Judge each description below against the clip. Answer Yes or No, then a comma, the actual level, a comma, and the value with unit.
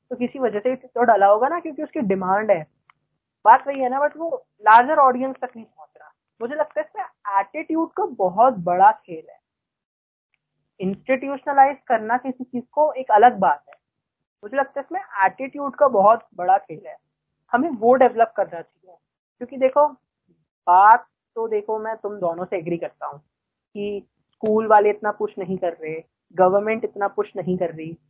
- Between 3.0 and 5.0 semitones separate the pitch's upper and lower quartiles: No, wide, 5.5 semitones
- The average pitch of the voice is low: No, high, 230 Hz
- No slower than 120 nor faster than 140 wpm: No, average, 180 wpm